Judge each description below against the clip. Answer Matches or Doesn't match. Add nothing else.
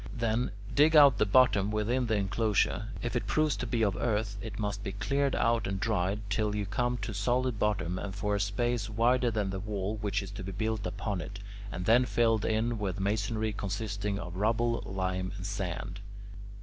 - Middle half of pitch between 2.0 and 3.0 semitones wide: Matches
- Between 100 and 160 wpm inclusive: Doesn't match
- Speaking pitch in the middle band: Doesn't match